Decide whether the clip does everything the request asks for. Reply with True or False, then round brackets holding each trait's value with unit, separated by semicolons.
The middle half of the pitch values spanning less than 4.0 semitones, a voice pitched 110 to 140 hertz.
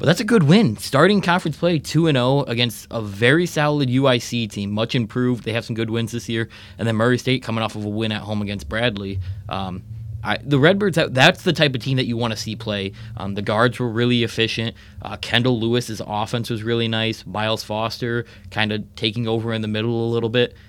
True (2.7 semitones; 115 Hz)